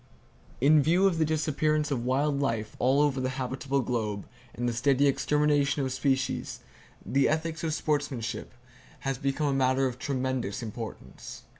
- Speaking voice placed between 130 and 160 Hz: Yes, low, 135 Hz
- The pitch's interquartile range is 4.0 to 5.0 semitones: No, narrow, 2.6 semitones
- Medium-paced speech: Yes, average, 155 wpm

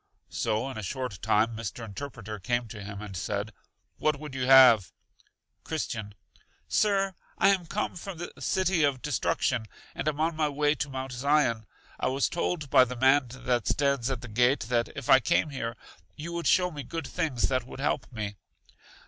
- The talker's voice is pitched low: Yes, low, 130 Hz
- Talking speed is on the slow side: No, average, 190 wpm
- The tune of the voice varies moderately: Yes, average, 4.6 semitones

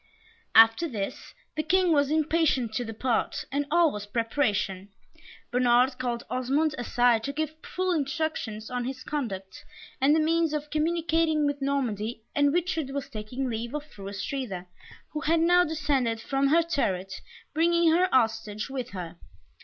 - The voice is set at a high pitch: Yes, very high, 275 Hz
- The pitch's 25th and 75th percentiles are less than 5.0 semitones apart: No, wide, 5.6 semitones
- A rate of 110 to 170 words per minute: Yes, average, 155 wpm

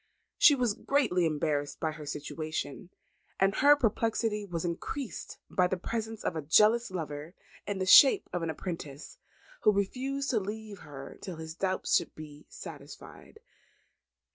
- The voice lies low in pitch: No, medium, 185 Hz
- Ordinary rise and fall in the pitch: No, wide, 6.1 semitones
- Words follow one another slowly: No, average, 150 wpm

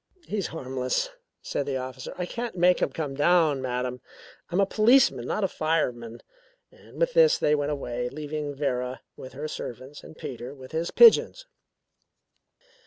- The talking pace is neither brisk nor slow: Yes, average, 160 wpm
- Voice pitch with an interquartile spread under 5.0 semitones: No, wide, 5.6 semitones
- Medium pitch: Yes, medium, 145 Hz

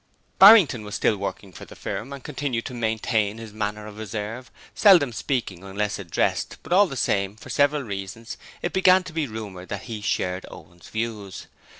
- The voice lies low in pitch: Yes, low, 110 Hz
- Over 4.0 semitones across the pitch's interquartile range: Yes, average, 5.3 semitones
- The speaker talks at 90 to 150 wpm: No, average, 185 wpm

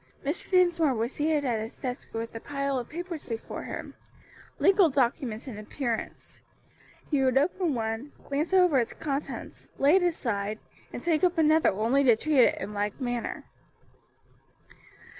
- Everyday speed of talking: Yes, average, 160 wpm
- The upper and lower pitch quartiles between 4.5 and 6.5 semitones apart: Yes, wide, 5.5 semitones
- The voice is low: No, very high, 275 Hz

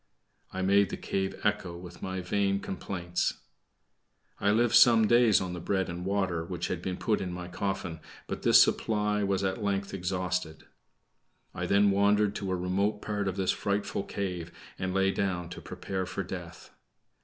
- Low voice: Yes, very low, 95 Hz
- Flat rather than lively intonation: Yes, narrow, 2.0 semitones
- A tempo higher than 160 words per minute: Yes, average, 175 wpm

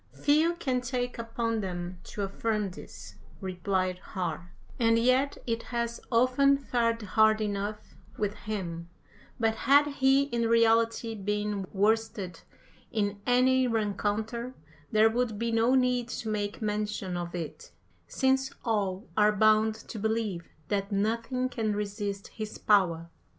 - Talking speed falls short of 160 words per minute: Yes, slow, 135 wpm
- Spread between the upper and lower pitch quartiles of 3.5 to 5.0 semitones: No, average, 2.8 semitones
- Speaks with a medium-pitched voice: No, high, 220 Hz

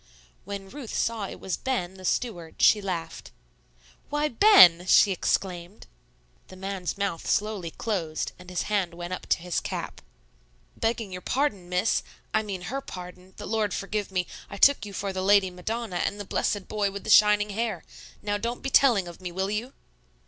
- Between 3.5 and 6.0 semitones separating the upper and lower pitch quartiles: No, average, 3.1 semitones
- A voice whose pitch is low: No, high, 200 Hz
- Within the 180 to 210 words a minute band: Yes, average, 185 wpm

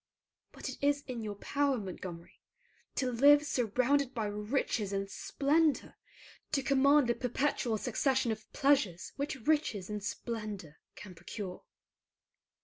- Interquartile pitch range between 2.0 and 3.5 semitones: No, average, 5.2 semitones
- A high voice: Yes, high, 240 Hz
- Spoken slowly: Yes, slow, 130 wpm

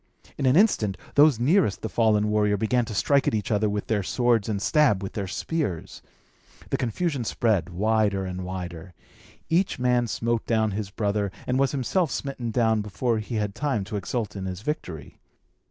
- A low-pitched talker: Yes, low, 110 Hz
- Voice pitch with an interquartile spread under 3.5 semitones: No, average, 3.9 semitones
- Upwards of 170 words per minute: Yes, average, 185 wpm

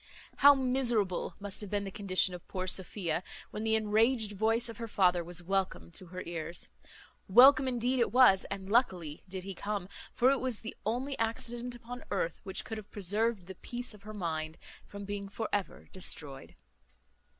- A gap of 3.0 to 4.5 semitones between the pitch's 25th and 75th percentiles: Yes, average, 4.1 semitones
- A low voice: No, high, 205 Hz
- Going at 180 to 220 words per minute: Yes, average, 185 wpm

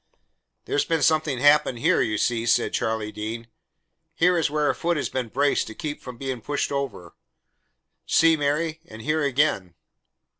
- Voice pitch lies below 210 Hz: Yes, medium, 140 Hz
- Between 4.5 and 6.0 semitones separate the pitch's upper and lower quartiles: Yes, average, 4.9 semitones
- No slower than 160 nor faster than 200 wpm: Yes, average, 165 wpm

